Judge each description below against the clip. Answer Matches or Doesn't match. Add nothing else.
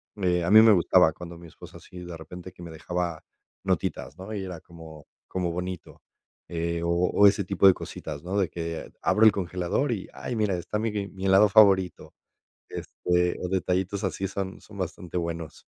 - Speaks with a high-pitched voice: Doesn't match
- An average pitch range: Doesn't match